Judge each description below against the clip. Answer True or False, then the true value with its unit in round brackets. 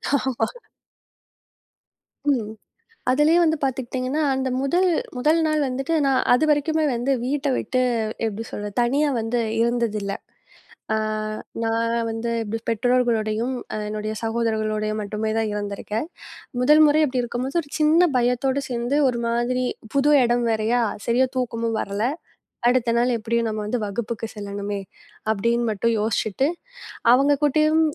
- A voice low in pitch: False (240 Hz)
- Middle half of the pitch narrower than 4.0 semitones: True (3.6 semitones)